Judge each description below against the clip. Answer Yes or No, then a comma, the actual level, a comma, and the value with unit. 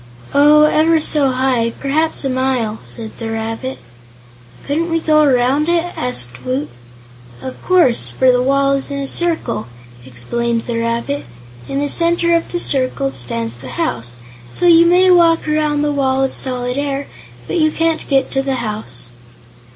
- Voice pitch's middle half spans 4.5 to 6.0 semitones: Yes, average, 4.9 semitones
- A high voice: Yes, very high, 270 Hz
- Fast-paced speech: No, average, 165 wpm